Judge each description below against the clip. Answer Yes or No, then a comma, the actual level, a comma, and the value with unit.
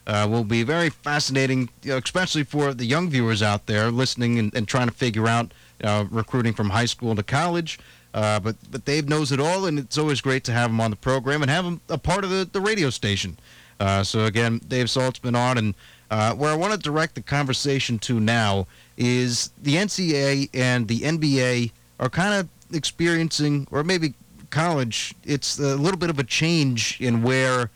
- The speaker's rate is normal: No, fast, 210 wpm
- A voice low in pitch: Yes, low, 130 Hz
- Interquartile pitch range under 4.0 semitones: No, average, 4.5 semitones